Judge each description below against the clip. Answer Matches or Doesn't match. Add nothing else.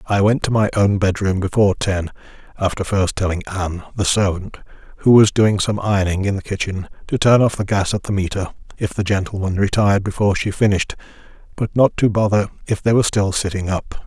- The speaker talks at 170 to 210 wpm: Matches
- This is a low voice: Matches